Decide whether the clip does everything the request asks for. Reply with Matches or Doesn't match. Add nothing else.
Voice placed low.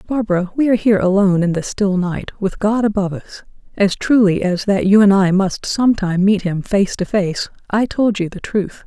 Doesn't match